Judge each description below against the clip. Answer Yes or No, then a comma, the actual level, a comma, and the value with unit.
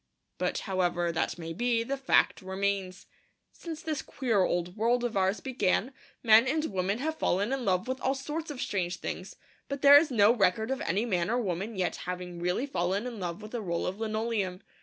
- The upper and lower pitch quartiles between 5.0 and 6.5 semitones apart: Yes, wide, 5.4 semitones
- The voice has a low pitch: No, high, 210 Hz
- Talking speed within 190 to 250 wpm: Yes, average, 200 wpm